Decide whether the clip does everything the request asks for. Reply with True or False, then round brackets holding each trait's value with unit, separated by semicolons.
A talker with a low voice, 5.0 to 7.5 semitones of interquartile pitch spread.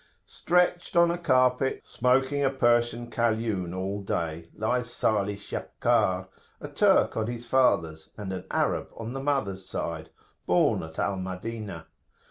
True (110 Hz; 5.4 semitones)